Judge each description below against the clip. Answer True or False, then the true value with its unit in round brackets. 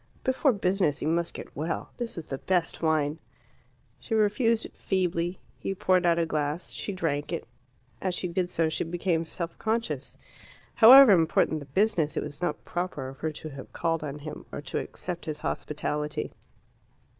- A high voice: False (170 Hz)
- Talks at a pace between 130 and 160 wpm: False (180 wpm)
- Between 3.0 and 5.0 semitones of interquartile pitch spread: True (3.7 semitones)